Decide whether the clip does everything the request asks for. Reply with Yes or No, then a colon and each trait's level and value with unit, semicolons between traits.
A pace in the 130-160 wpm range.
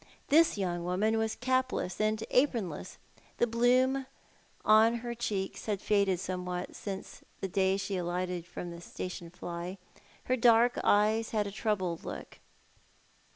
Yes: average, 140 wpm